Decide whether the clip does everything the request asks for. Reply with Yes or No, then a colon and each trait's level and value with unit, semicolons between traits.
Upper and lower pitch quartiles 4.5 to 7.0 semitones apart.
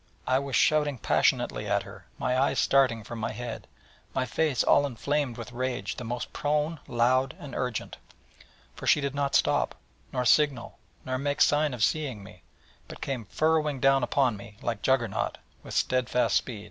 No: average, 3.1 semitones